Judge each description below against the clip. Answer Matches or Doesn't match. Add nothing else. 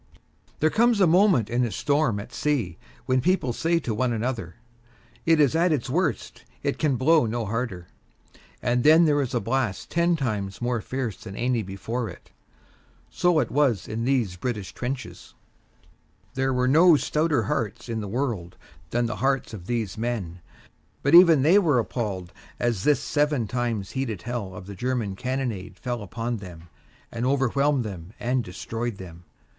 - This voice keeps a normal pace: Matches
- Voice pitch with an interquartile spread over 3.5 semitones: Matches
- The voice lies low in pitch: Matches